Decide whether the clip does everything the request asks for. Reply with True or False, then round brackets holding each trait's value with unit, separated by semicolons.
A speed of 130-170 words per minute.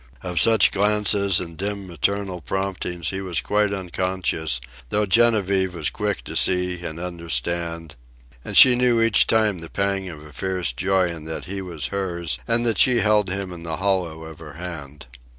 False (180 wpm)